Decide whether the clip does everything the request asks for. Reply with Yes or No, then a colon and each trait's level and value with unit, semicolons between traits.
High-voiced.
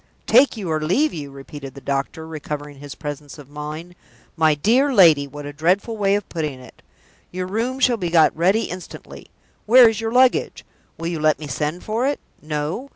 No: medium, 160 Hz